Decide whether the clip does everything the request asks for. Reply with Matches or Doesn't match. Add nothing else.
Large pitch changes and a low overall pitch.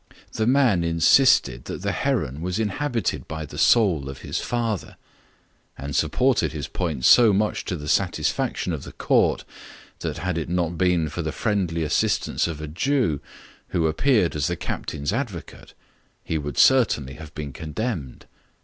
Matches